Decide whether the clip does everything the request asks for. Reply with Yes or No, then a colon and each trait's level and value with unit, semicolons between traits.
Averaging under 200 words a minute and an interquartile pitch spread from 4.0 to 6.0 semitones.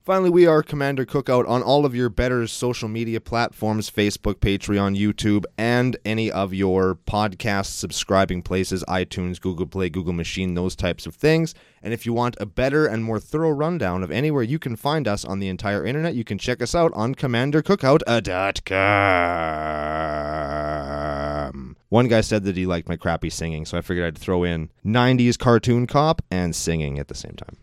Yes: average, 180 wpm; average, 5.2 semitones